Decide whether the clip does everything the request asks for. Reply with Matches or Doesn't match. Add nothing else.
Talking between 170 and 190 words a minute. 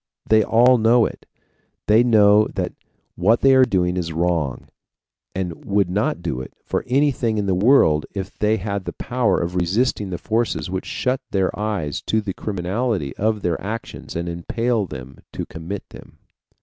Matches